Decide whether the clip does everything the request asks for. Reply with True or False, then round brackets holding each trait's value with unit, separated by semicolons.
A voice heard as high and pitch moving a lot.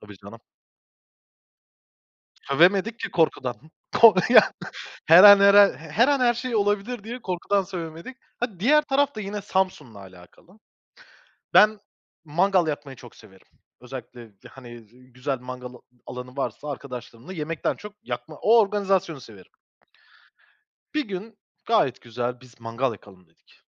False (165 Hz; 8.7 semitones)